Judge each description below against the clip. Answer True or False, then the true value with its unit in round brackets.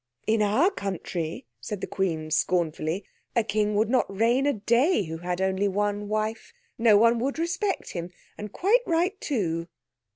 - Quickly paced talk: False (165 wpm)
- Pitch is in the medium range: False (210 Hz)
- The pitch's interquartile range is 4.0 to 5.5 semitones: True (4.6 semitones)